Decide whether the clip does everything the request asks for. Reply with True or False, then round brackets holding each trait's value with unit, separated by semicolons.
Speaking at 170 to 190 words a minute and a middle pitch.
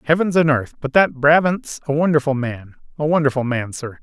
True (180 wpm; 145 Hz)